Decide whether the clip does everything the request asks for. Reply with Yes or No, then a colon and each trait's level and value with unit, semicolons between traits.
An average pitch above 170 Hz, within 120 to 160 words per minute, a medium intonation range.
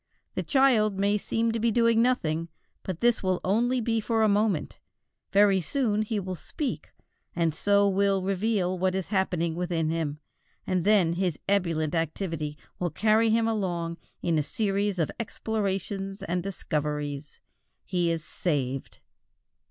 Yes: high, 190 Hz; average, 150 wpm; average, 4.2 semitones